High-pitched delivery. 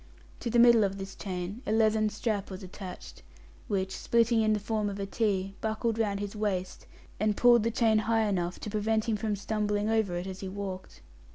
Yes: high, 210 Hz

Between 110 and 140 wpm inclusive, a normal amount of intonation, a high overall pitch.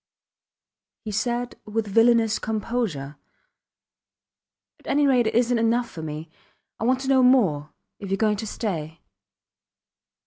Yes: slow, 135 wpm; average, 4.0 semitones; high, 225 Hz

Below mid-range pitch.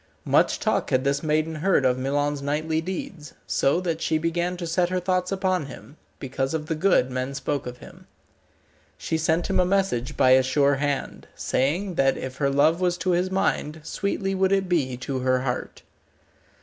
No: medium, 155 Hz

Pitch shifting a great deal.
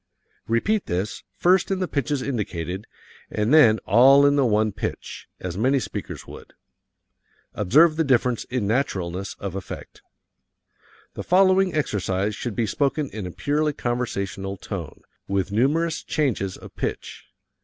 Yes: wide, 6.7 semitones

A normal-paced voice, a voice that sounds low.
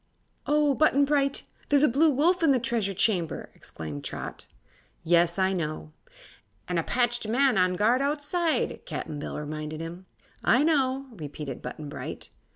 No: average, 155 wpm; high, 230 Hz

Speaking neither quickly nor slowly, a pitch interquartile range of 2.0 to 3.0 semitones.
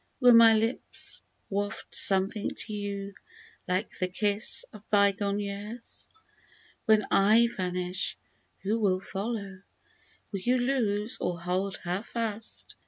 No: slow, 120 wpm; narrow, 2.5 semitones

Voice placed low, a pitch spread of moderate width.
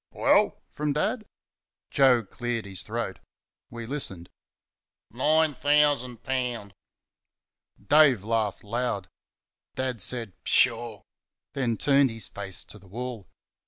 Yes: low, 120 Hz; average, 4.2 semitones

